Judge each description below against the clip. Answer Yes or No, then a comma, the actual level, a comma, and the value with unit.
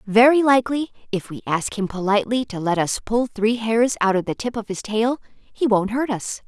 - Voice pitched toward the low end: No, high, 220 Hz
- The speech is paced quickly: Yes, fast, 220 wpm